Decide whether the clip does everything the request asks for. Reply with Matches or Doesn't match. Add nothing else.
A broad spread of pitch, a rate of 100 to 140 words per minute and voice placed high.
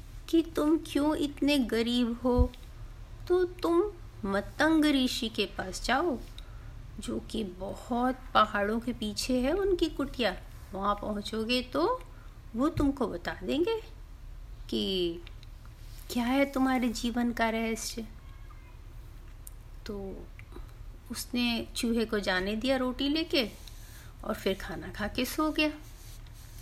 Matches